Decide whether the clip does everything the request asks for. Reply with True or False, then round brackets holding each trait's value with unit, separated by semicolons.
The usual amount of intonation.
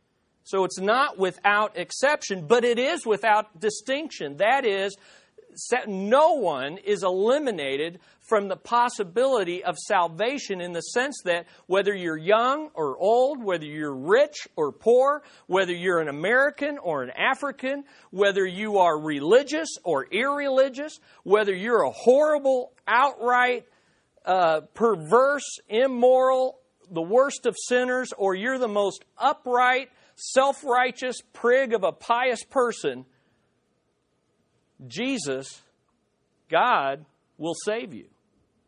False (5.8 semitones)